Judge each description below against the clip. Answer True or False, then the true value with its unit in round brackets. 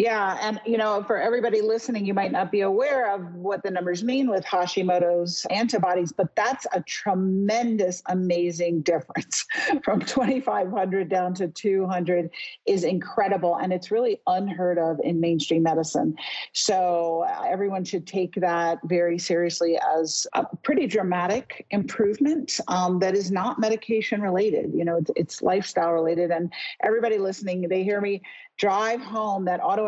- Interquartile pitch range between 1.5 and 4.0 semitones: True (3.7 semitones)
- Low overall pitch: False (190 Hz)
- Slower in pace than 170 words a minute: True (155 wpm)